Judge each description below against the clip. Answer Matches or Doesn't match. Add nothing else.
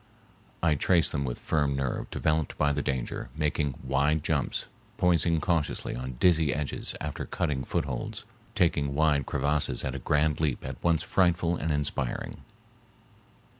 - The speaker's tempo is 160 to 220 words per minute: Doesn't match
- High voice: Doesn't match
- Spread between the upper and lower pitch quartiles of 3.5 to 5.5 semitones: Doesn't match